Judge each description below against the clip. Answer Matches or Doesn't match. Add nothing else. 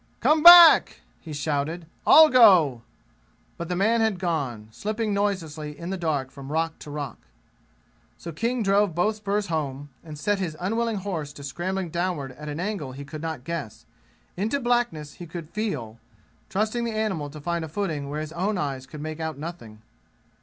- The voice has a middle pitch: Matches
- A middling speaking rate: Matches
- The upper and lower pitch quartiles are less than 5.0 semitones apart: Doesn't match